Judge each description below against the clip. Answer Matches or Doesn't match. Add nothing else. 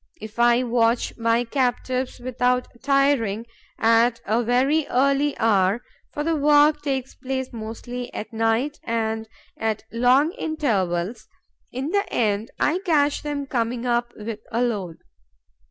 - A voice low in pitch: Doesn't match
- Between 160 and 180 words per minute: Doesn't match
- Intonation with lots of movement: Doesn't match